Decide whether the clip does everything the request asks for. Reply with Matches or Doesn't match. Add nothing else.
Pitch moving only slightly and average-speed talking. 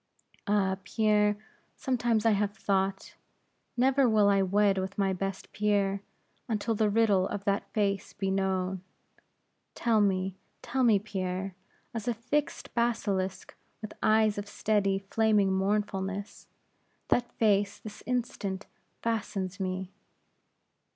Doesn't match